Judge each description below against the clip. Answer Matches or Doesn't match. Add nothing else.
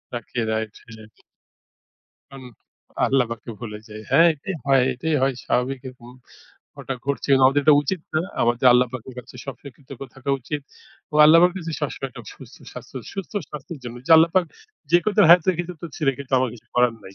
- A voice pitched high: Doesn't match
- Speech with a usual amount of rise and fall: Matches